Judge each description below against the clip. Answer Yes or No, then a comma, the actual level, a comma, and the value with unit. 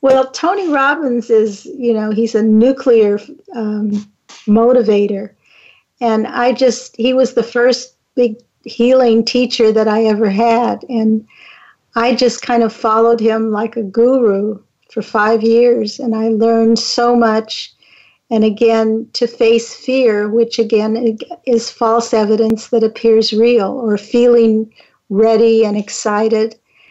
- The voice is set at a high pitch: Yes, high, 230 Hz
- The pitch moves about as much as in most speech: No, narrow, 1.6 semitones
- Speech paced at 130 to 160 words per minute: Yes, slow, 135 wpm